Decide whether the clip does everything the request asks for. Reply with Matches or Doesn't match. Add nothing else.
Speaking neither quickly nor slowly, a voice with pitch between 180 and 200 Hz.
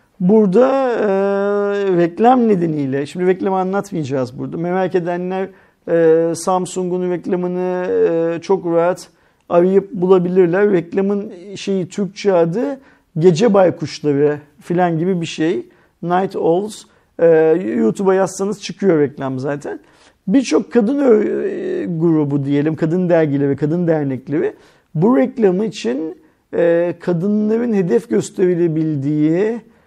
Matches